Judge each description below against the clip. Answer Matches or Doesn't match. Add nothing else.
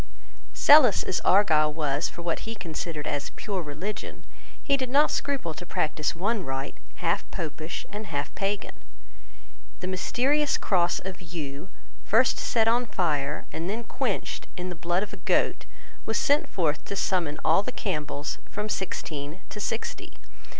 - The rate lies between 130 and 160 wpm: Matches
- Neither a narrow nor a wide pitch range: Doesn't match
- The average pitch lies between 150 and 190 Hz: Matches